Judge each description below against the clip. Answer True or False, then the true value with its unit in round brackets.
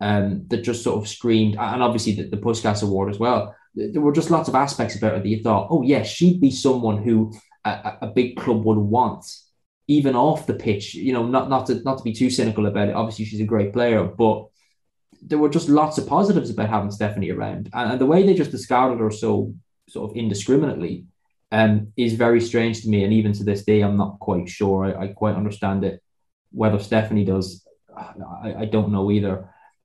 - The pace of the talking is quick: True (220 wpm)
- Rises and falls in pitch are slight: False (3.2 semitones)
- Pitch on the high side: False (110 Hz)